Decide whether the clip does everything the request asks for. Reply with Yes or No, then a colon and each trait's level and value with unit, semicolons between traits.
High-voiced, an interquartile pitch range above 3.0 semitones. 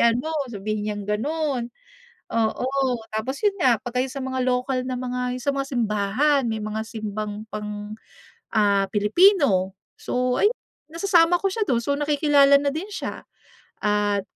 Yes: very high, 250 Hz; average, 4.8 semitones